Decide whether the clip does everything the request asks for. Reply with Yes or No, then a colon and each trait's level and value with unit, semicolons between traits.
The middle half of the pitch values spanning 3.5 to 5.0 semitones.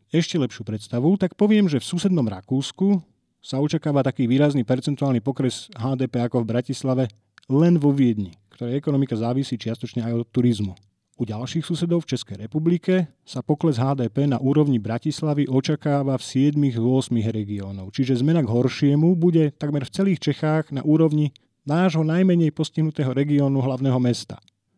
Yes: average, 4.1 semitones